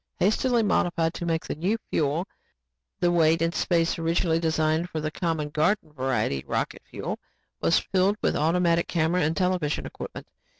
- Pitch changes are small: Yes, narrow, 2.2 semitones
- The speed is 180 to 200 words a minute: No, average, 165 wpm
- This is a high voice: No, medium, 165 Hz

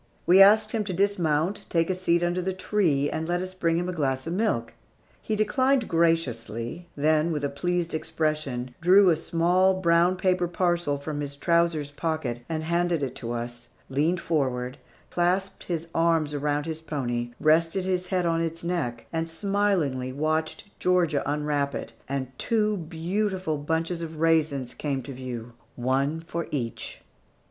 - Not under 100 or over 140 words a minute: No, average, 165 wpm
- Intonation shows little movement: No, average, 3.9 semitones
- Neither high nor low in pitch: Yes, medium, 165 Hz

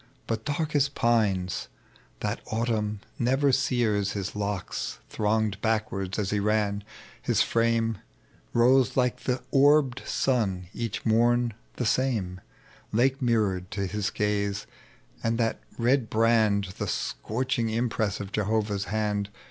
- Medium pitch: No, low, 110 Hz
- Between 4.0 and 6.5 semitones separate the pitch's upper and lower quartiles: No, average, 3.0 semitones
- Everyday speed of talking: No, slow, 125 wpm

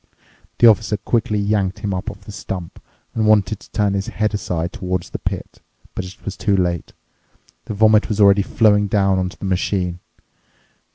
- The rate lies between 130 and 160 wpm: No, average, 180 wpm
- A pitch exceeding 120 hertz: No, low, 100 Hz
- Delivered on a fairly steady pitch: Yes, narrow, 2.3 semitones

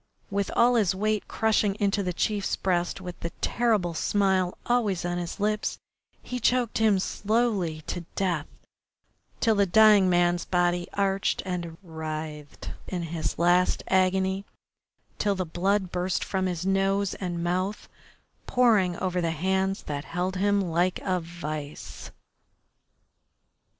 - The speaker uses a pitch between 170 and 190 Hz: Yes, medium, 185 Hz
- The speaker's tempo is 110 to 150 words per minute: Yes, slow, 135 wpm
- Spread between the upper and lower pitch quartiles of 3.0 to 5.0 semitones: No, narrow, 2.6 semitones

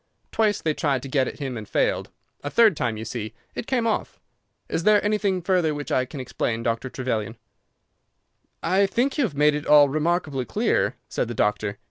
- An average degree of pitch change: No, wide, 7.5 semitones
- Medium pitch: Yes, medium, 145 Hz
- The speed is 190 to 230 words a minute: Yes, average, 195 wpm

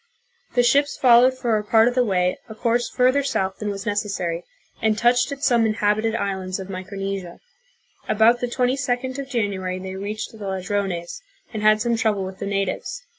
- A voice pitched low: No, high, 215 Hz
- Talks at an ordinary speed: Yes, average, 180 wpm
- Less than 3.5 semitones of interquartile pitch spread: No, average, 3.8 semitones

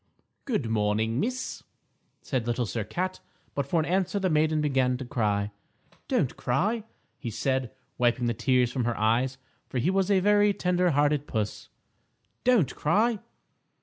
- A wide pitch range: Yes, wide, 7.6 semitones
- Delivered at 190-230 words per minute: No, average, 155 wpm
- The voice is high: No, low, 135 Hz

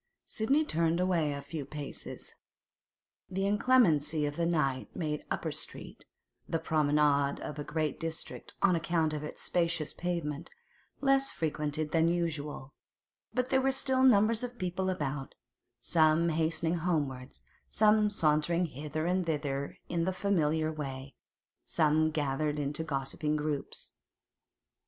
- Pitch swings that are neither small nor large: Yes, average, 3.3 semitones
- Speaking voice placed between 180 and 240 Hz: No, medium, 160 Hz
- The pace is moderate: No, slow, 130 wpm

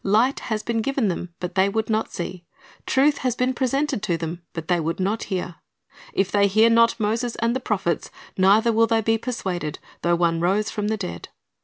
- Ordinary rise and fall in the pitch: Yes, average, 4.5 semitones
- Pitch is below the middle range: No, high, 210 Hz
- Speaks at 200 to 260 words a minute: Yes, fast, 205 wpm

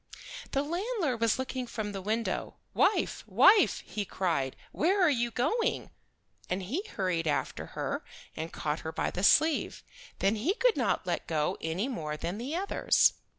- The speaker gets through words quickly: No, average, 165 wpm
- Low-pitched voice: No, high, 230 Hz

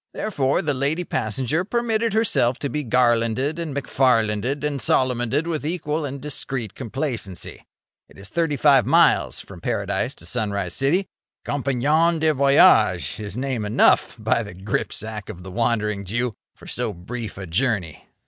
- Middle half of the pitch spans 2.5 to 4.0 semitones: No, wide, 5.4 semitones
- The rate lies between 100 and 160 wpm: Yes, average, 150 wpm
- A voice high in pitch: No, low, 130 Hz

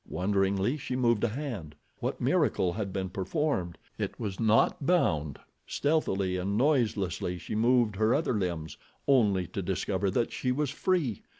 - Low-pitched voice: Yes, low, 105 Hz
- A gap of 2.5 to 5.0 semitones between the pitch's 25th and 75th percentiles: No, wide, 5.4 semitones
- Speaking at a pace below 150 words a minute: No, average, 155 wpm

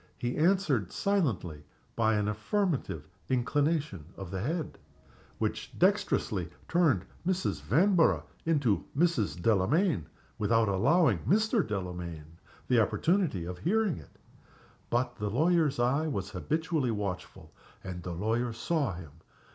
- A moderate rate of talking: No, slow, 125 wpm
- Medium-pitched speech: No, low, 120 Hz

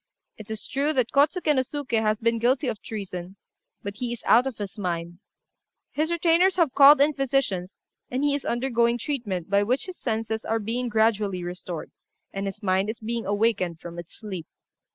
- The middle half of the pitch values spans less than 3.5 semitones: No, average, 5.2 semitones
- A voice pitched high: Yes, high, 225 Hz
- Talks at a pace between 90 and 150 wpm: No, average, 190 wpm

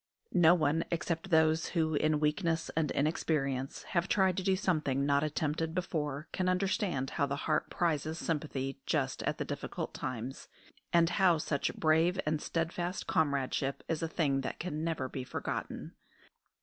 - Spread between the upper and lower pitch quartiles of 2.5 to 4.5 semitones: Yes, average, 3.1 semitones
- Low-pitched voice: No, medium, 160 Hz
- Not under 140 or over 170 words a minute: Yes, average, 160 wpm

